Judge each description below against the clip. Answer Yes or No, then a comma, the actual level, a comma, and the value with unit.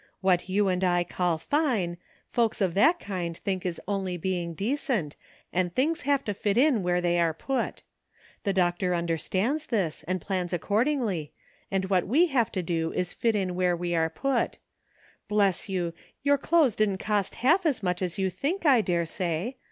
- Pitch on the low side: No, high, 190 Hz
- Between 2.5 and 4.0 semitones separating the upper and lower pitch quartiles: No, average, 5.0 semitones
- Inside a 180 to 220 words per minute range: Yes, average, 185 wpm